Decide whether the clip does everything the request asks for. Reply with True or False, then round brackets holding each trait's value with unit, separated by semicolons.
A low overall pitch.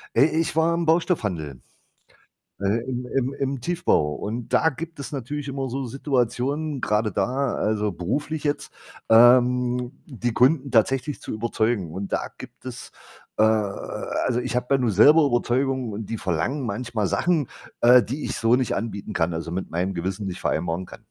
True (120 Hz)